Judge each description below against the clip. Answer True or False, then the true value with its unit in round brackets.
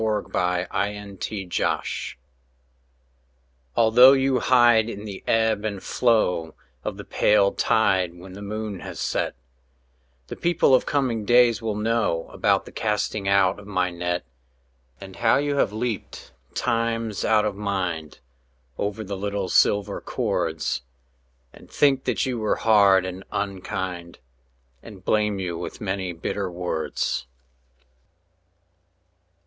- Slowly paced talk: True (130 wpm)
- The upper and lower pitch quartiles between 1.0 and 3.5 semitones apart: True (3.2 semitones)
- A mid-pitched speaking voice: False (105 Hz)